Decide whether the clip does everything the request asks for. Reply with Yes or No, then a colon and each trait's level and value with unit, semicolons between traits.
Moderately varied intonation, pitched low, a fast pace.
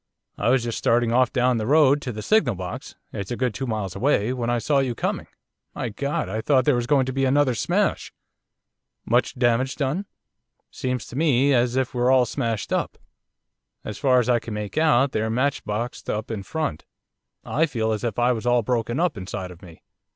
Yes: average, 3.2 semitones; low, 125 Hz; fast, 210 wpm